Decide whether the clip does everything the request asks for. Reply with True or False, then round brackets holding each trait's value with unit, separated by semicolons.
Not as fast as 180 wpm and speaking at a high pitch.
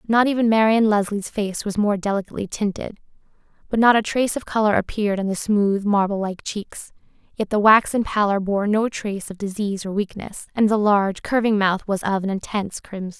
False (195 wpm; 205 Hz)